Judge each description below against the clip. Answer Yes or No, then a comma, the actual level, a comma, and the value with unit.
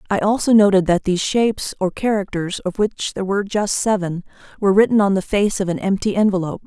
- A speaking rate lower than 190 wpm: No, fast, 205 wpm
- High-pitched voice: Yes, high, 195 Hz